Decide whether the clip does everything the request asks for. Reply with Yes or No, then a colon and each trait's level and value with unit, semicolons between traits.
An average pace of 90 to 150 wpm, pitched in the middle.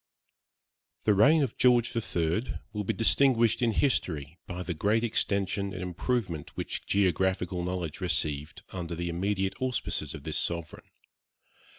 No: average, 140 wpm; very low, 95 Hz